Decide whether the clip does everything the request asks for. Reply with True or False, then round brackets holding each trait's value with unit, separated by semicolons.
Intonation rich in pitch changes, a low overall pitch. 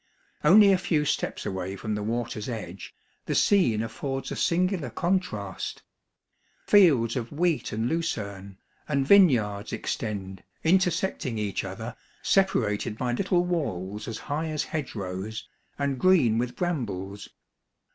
True (8.2 semitones; 120 Hz)